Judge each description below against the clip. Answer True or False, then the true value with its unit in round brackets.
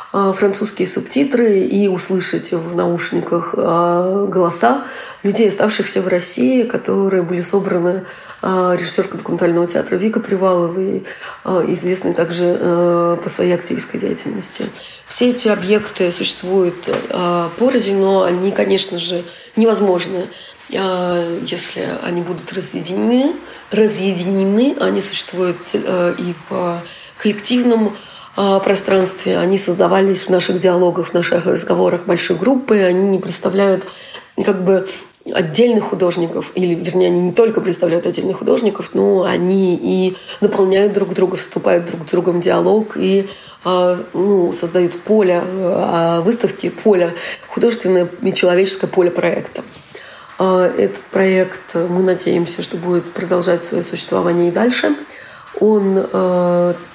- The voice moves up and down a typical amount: False (2.0 semitones)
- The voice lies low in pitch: False (185 Hz)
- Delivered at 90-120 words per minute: True (115 wpm)